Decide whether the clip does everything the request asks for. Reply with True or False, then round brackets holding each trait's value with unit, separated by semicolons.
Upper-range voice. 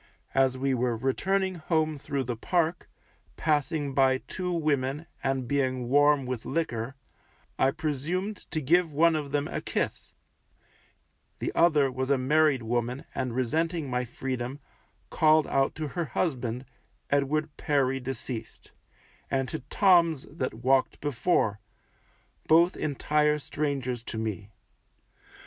False (140 Hz)